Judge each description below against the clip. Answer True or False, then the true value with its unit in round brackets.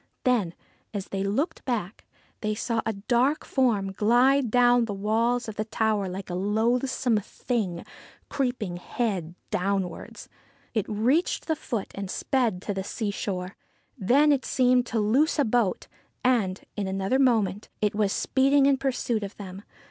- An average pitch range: True (4.1 semitones)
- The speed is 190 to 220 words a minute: False (155 wpm)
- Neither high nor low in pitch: False (220 Hz)